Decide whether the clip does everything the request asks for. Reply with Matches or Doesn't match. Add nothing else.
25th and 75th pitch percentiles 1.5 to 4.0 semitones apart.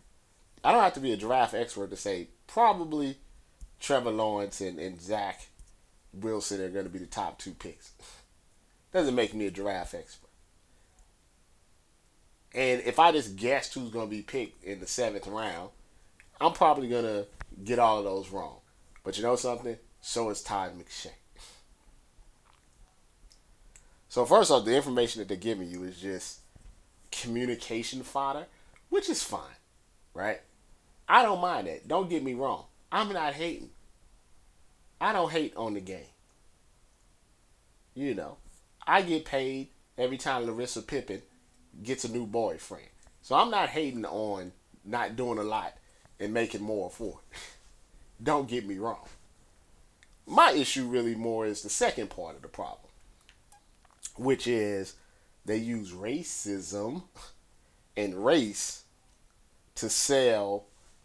Doesn't match